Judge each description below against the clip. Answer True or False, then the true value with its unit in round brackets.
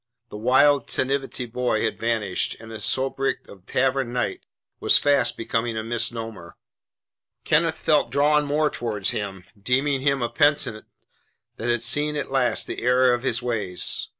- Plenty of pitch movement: False (3.6 semitones)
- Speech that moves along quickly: False (155 wpm)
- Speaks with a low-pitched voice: True (125 Hz)